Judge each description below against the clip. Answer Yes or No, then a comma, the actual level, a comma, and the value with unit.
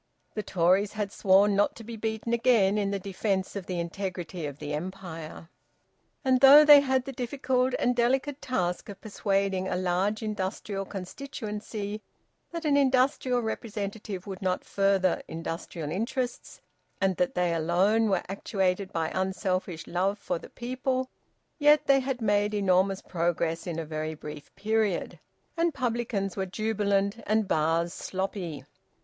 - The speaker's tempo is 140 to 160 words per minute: Yes, average, 150 wpm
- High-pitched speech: Yes, high, 200 Hz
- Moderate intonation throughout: Yes, average, 4.2 semitones